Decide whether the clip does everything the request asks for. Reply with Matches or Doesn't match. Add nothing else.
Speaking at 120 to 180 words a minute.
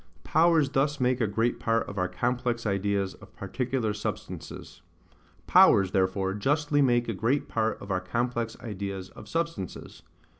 Matches